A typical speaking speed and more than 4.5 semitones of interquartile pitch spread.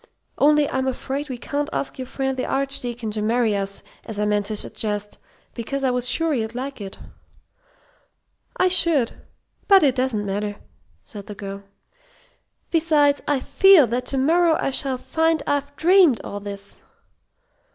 Yes: average, 160 wpm; average, 5.3 semitones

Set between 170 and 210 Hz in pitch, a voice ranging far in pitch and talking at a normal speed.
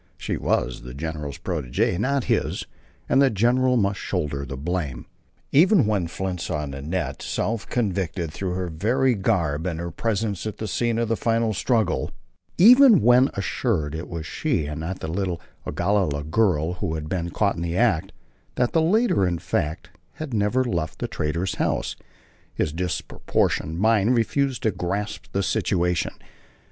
No: very low, 95 Hz; wide, 6.2 semitones; average, 165 wpm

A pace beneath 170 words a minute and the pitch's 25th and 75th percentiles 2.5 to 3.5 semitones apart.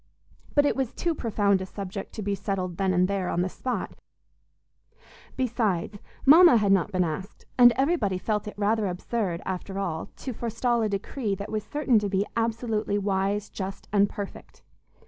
No: average, 175 wpm; average, 3.2 semitones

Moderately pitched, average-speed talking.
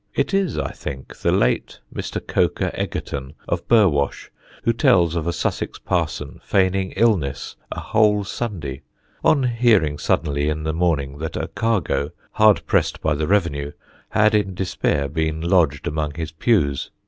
No: very low, 85 Hz; average, 155 wpm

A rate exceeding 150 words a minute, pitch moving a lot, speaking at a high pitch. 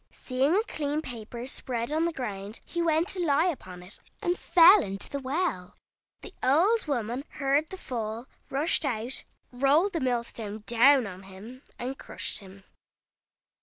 Yes: average, 165 wpm; wide, 5.9 semitones; very high, 265 Hz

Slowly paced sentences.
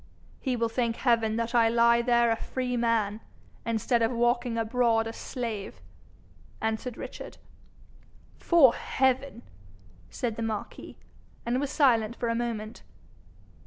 Yes: slow, 130 wpm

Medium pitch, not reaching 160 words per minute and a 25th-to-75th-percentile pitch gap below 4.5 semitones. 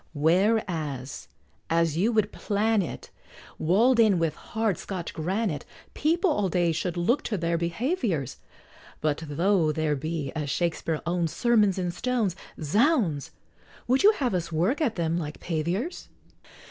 No: medium, 175 Hz; average, 145 wpm; wide, 5.5 semitones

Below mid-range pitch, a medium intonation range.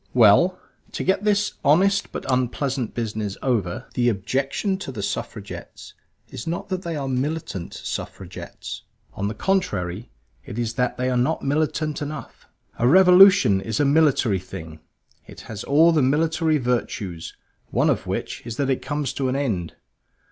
No: low, 130 Hz; wide, 6.1 semitones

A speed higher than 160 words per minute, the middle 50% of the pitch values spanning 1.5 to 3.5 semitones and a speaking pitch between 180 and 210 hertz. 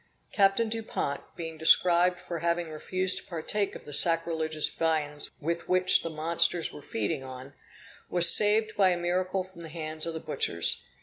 No: average, 170 wpm; average, 2.7 semitones; medium, 170 Hz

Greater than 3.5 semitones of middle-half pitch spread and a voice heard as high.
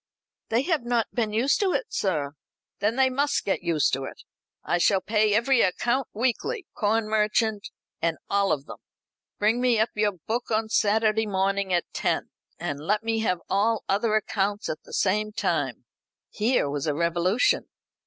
No: average, 3.2 semitones; high, 215 Hz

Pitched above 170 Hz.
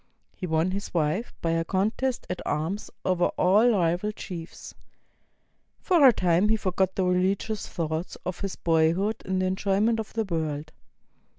Yes: medium, 185 Hz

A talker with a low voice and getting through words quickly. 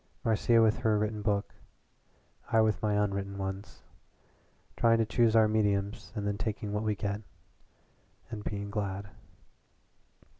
No: low, 105 Hz; average, 140 wpm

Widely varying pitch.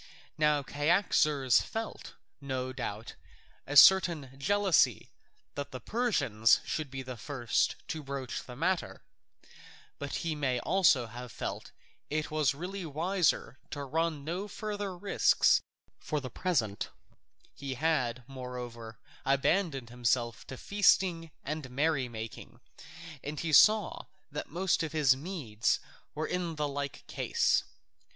No: average, 4.8 semitones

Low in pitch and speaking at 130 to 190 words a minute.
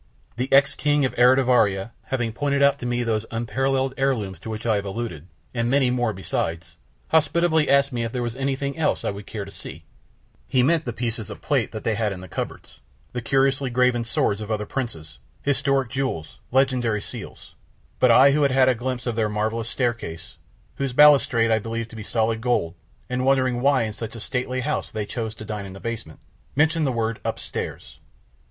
No: low, 120 Hz; fast, 205 wpm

